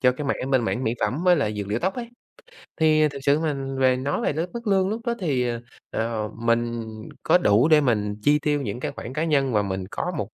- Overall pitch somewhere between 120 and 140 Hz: Yes, low, 135 Hz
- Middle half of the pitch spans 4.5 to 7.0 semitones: Yes, average, 5.0 semitones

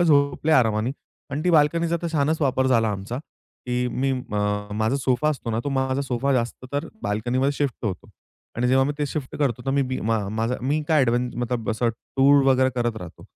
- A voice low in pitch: Yes, low, 130 Hz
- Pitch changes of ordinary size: Yes, average, 3.2 semitones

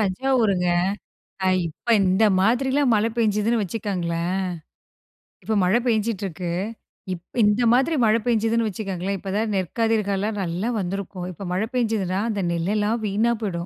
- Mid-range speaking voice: No, high, 210 Hz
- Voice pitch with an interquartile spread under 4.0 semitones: Yes, average, 3.4 semitones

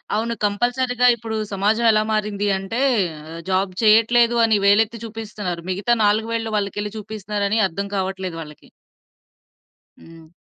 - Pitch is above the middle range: Yes, high, 210 Hz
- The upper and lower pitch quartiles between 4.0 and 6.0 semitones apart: No, narrow, 2.6 semitones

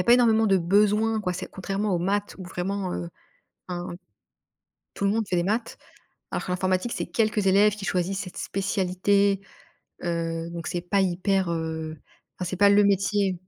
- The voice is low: No, high, 195 Hz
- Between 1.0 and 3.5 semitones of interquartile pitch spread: Yes, narrow, 2.4 semitones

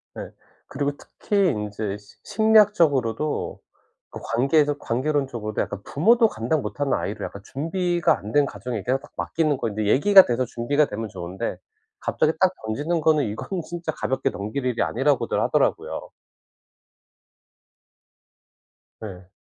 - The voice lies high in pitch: No, low, 135 Hz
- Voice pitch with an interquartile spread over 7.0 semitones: No, wide, 6.6 semitones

